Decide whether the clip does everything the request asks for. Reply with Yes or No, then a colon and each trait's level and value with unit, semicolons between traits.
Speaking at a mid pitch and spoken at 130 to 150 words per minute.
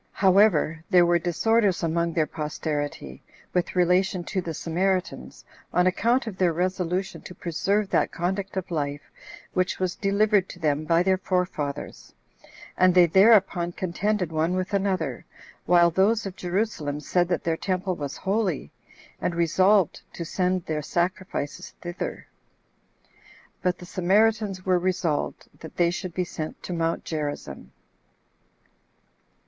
Yes: medium, 180 Hz; average, 140 wpm